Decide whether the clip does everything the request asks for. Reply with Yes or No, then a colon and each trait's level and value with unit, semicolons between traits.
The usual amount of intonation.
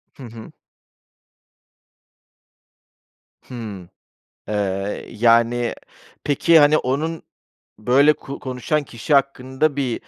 Yes: average, 3.8 semitones